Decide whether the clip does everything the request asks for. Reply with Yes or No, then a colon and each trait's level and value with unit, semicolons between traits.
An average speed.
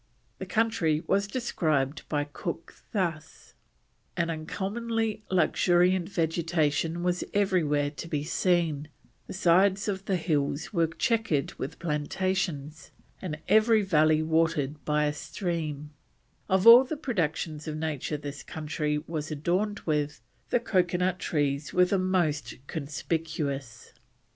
No: slow, 125 wpm